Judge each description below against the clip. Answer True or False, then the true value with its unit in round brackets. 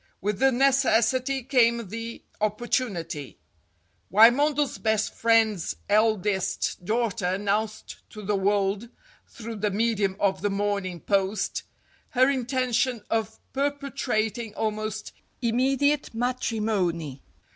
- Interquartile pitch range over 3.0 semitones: True (3.4 semitones)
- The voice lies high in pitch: True (220 Hz)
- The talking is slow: True (105 wpm)